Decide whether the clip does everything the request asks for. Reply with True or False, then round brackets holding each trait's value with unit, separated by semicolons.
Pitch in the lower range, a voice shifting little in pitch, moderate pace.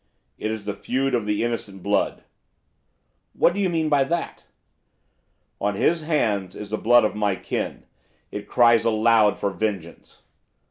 False (110 Hz; 4.1 semitones; 155 wpm)